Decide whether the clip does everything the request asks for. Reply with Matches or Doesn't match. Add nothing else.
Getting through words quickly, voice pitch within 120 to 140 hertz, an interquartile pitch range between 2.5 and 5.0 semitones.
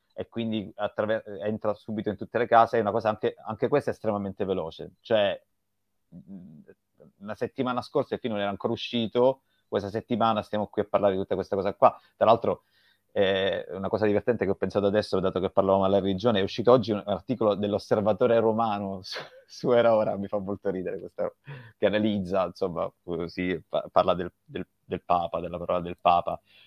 Doesn't match